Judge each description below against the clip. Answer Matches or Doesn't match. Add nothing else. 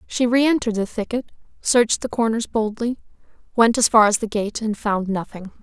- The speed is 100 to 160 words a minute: Doesn't match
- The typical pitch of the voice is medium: Doesn't match